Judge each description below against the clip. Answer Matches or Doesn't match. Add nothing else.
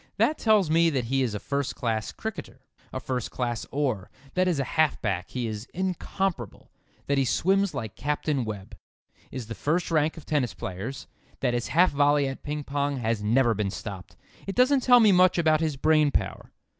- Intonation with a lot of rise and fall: Matches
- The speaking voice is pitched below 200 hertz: Matches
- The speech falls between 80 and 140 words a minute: Doesn't match